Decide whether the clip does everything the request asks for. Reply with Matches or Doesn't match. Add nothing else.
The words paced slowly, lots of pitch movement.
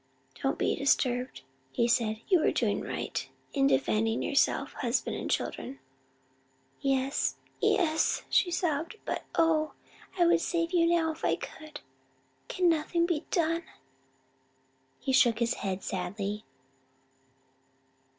Matches